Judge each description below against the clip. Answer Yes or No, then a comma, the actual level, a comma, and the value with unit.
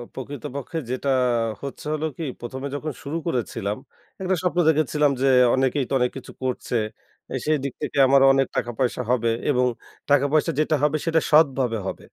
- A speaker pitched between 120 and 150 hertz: Yes, medium, 140 Hz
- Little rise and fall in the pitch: No, average, 3.2 semitones